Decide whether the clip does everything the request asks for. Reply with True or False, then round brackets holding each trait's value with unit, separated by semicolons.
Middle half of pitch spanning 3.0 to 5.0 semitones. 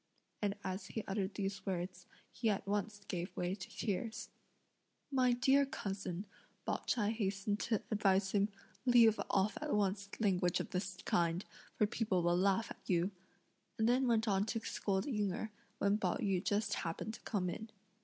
False (2.6 semitones)